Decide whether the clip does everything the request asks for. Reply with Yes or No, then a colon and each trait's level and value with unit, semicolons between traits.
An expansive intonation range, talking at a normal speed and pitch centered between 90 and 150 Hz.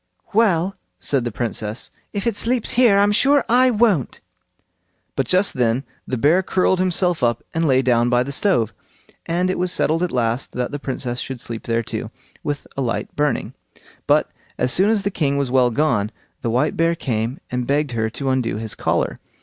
Yes: wide, 7.2 semitones; average, 195 wpm; medium, 140 Hz